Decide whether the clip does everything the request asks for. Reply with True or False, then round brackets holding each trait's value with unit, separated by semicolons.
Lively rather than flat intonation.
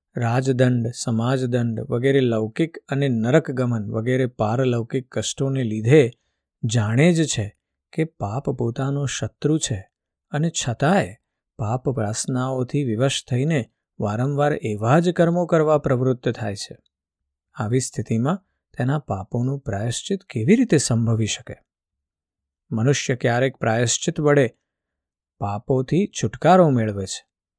False (4.3 semitones)